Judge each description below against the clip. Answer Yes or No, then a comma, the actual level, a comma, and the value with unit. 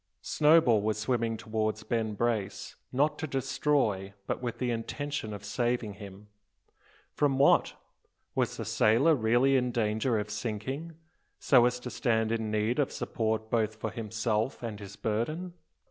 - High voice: No, low, 115 Hz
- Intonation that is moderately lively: Yes, average, 3.3 semitones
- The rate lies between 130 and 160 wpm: Yes, average, 150 wpm